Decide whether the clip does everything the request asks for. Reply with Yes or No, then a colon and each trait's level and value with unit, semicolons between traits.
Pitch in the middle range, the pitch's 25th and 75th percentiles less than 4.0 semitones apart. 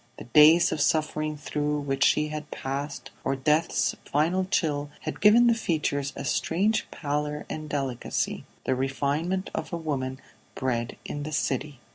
Yes: medium, 150 Hz; narrow, 2.4 semitones